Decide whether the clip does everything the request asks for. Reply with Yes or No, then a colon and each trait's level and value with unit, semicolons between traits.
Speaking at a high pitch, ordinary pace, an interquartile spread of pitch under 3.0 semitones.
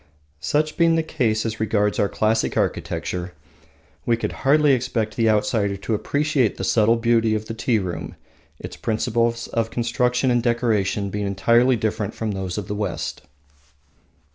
No: low, 115 Hz; average, 160 wpm; narrow, 2.6 semitones